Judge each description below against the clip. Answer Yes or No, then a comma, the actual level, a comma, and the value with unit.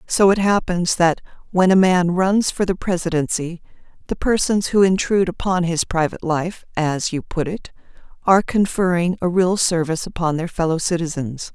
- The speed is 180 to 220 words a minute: No, average, 165 wpm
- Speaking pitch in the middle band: Yes, medium, 175 Hz